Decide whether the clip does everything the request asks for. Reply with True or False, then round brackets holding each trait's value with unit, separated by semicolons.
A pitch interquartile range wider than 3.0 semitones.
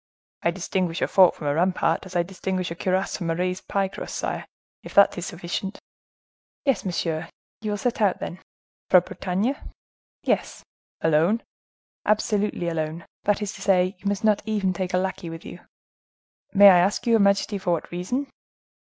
False (2.6 semitones)